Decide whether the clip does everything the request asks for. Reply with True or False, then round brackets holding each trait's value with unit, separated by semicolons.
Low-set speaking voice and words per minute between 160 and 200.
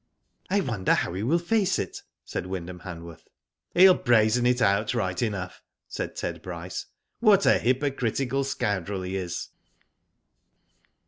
False (110 Hz; 150 wpm)